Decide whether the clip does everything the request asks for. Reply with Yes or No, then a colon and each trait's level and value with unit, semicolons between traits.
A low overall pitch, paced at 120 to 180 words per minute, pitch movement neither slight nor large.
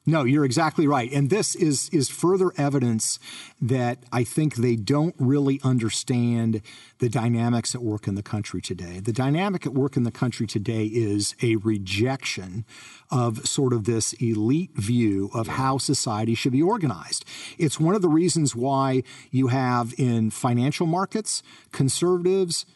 Yes: low, 130 Hz; average, 160 wpm; average, 3.9 semitones